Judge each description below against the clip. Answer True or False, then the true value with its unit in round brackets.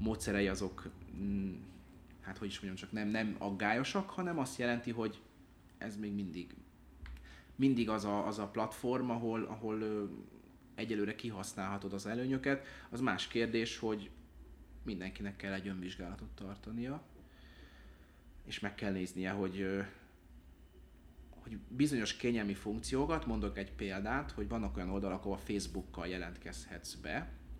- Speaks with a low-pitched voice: True (100 Hz)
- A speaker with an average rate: True (130 wpm)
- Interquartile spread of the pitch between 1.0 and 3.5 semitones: False (3.9 semitones)